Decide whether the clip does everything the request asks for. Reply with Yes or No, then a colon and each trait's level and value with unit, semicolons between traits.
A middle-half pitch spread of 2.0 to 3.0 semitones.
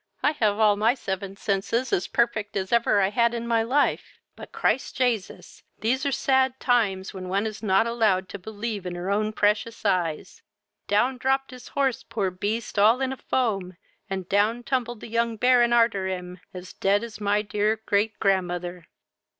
No: average, 3.4 semitones